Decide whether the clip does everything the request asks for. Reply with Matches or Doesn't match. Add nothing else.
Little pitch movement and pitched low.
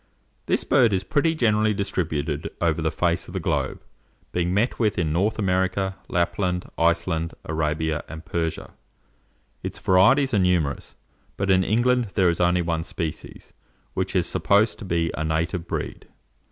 Doesn't match